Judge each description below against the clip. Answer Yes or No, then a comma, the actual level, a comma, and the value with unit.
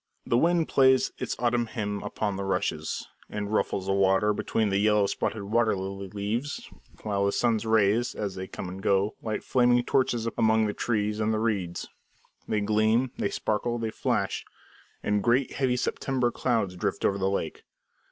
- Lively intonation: No, average, 3.1 semitones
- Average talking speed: Yes, average, 170 wpm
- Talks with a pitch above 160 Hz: No, low, 105 Hz